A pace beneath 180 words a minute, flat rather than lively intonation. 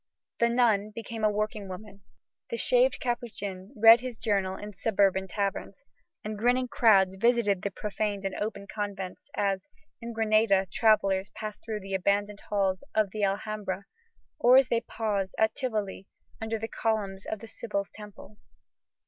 Yes: average, 155 wpm; narrow, 2.3 semitones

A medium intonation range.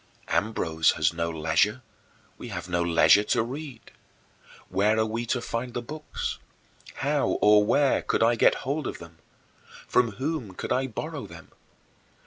No: wide, 6.5 semitones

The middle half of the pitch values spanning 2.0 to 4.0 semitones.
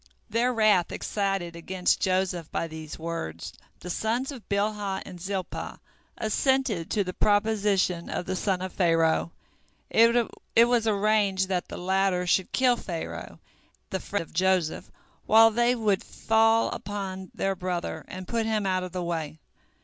Yes: average, 3.4 semitones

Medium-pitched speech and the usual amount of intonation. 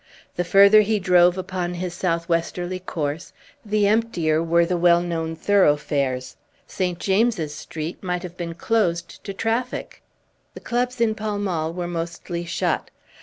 Yes: medium, 175 Hz; average, 3.1 semitones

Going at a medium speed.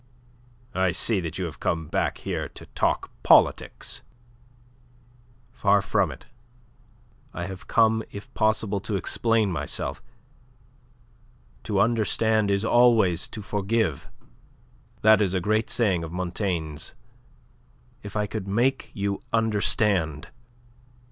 No: slow, 115 wpm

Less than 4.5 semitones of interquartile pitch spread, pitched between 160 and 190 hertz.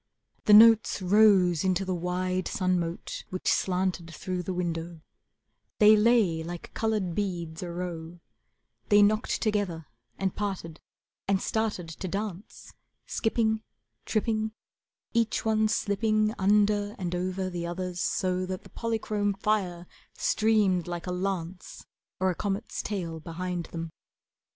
Yes: average, 3.1 semitones; medium, 185 Hz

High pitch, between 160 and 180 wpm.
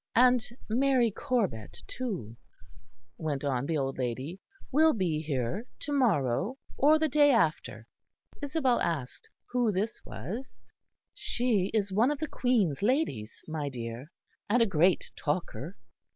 No: high, 195 Hz; slow, 135 wpm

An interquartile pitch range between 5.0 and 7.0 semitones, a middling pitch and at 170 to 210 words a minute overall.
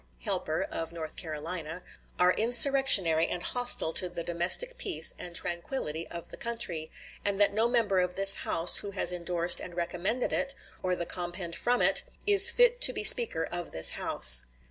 Yes: wide, 5.6 semitones; medium, 180 Hz; average, 175 wpm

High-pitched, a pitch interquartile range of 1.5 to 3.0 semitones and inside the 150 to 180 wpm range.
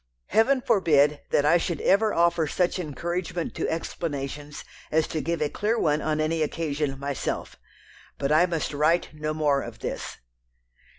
No: medium, 155 Hz; average, 2.7 semitones; average, 160 wpm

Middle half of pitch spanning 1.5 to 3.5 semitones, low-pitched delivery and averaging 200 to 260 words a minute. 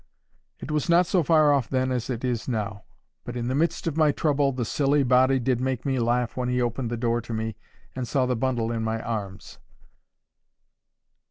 Yes: average, 2.8 semitones; low, 125 Hz; fast, 205 wpm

